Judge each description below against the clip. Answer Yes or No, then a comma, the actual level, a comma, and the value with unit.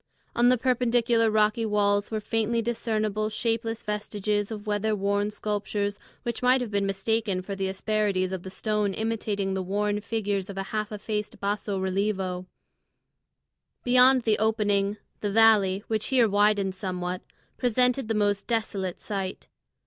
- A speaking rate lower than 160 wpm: Yes, average, 150 wpm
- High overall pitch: Yes, high, 210 Hz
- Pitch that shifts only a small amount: Yes, narrow, 2.1 semitones